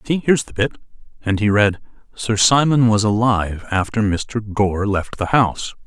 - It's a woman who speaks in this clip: No, male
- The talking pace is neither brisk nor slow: Yes, average, 175 wpm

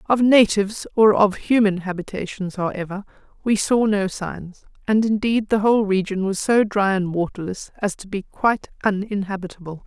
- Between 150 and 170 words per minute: Yes, average, 160 wpm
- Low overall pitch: No, high, 200 Hz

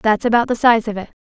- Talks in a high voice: Yes, high, 225 Hz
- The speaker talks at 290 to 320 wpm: Yes, fast, 295 wpm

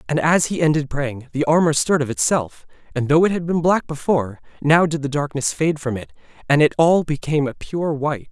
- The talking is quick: Yes, fast, 225 wpm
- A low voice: No, medium, 150 Hz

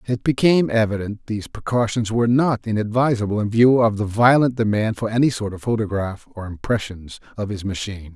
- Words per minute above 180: No, average, 175 wpm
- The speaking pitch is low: Yes, low, 110 Hz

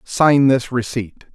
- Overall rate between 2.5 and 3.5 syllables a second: Yes, 3.4 syllables/s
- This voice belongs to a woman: No, male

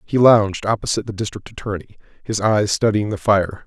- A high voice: No, low, 105 Hz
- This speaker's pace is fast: No, average, 180 wpm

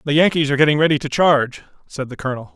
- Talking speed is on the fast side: Yes, fast, 235 wpm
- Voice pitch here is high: No, medium, 145 Hz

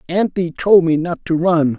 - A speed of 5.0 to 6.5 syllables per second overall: No, 4.6 syllables/s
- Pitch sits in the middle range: Yes, medium, 170 Hz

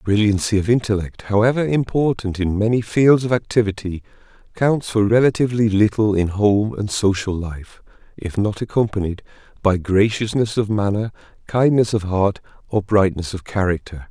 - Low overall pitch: Yes, low, 105 Hz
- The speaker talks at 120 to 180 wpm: Yes, slow, 135 wpm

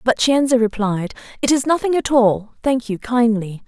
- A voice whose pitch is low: No, high, 235 Hz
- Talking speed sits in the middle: Yes, average, 180 wpm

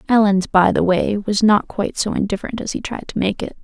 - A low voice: No, high, 205 Hz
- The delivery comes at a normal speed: No, fast, 250 wpm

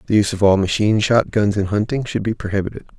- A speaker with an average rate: No, fast, 220 wpm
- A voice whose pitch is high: No, low, 105 Hz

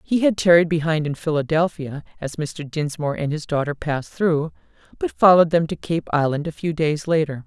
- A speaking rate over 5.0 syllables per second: Yes, 5.5 syllables/s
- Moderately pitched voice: Yes, medium, 160 Hz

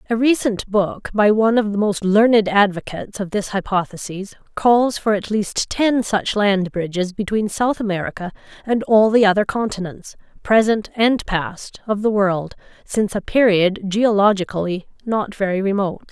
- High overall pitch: Yes, high, 205 Hz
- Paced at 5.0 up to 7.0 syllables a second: No, 4.8 syllables/s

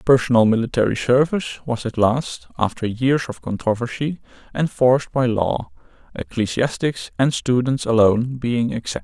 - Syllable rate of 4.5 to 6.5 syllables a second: Yes, 5.0 syllables/s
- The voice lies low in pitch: Yes, low, 120 Hz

